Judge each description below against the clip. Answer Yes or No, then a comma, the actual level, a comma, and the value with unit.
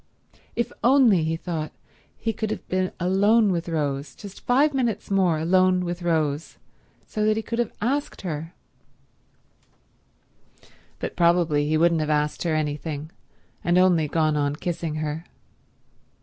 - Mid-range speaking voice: Yes, medium, 170 Hz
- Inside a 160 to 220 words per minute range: No, average, 145 wpm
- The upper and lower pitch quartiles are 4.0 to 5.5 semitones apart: Yes, average, 4.7 semitones